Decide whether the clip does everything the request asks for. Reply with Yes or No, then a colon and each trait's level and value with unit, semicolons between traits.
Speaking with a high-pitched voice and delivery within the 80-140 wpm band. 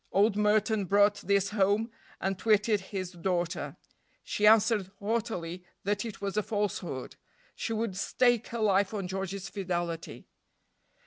Yes: high, 200 Hz; slow, 135 wpm